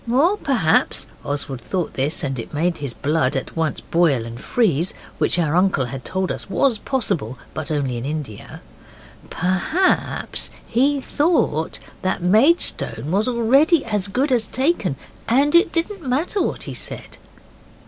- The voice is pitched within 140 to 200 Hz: Yes, medium, 185 Hz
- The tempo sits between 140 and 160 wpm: Yes, average, 150 wpm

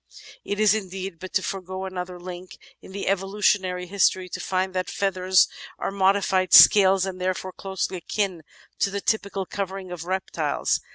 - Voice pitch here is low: No, high, 190 Hz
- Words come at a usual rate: Yes, average, 160 wpm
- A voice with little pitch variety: Yes, narrow, 1.1 semitones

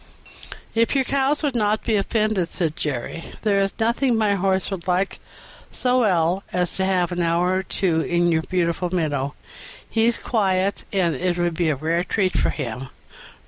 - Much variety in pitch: No, average, 4.0 semitones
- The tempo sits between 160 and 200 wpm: Yes, average, 180 wpm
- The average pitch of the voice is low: No, medium, 185 Hz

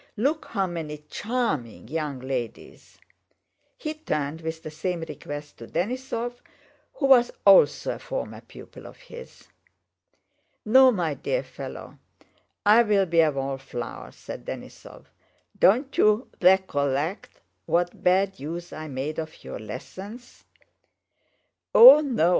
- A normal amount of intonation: No, wide, 8.0 semitones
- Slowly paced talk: Yes, slow, 120 wpm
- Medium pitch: Yes, medium, 175 Hz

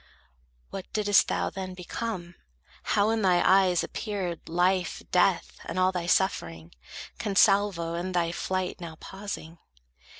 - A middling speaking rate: No, slow, 130 wpm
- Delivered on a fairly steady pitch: Yes, narrow, 2.2 semitones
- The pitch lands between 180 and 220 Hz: Yes, medium, 185 Hz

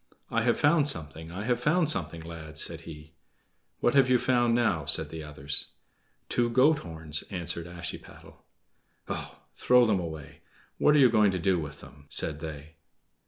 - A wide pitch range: Yes, wide, 7.3 semitones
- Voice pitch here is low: Yes, very low, 85 Hz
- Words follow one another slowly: No, average, 170 wpm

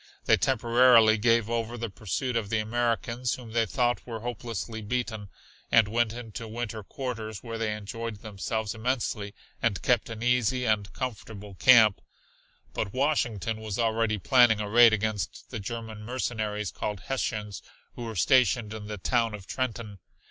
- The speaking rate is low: No, average, 160 wpm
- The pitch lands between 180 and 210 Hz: No, low, 115 Hz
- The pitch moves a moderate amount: No, narrow, 2.2 semitones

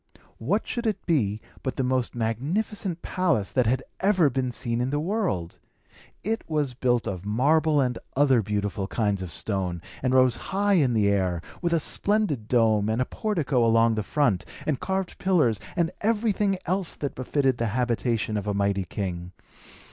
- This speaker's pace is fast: No, average, 175 wpm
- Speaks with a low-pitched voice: Yes, low, 125 Hz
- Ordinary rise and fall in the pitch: No, wide, 7.7 semitones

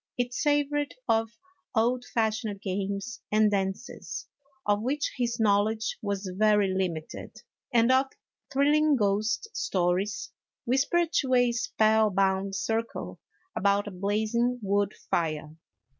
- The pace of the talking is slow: Yes, slow, 115 wpm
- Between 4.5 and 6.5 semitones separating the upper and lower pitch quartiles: No, average, 3.7 semitones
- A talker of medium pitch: No, high, 215 Hz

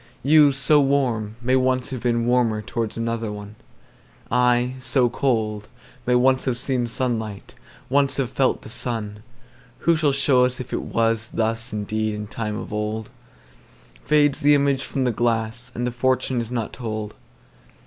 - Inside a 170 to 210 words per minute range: No, average, 140 wpm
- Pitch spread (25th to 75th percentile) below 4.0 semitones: Yes, average, 2.9 semitones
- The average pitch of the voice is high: No, low, 120 Hz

